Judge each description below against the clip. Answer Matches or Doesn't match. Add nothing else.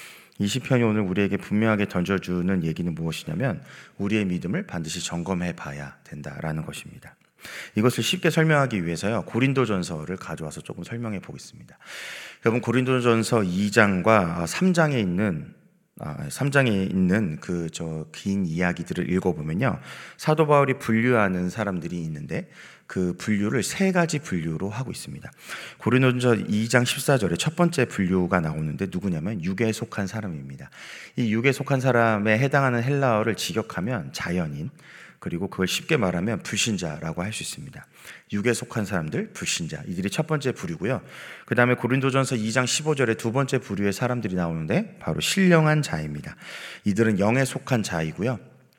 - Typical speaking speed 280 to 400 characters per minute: Matches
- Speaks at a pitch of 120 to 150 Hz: Doesn't match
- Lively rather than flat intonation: Matches